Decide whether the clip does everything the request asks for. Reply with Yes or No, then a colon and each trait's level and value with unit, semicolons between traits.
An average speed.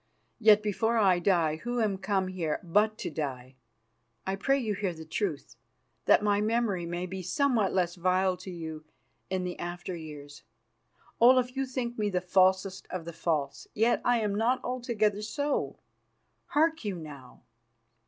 Yes: average, 165 wpm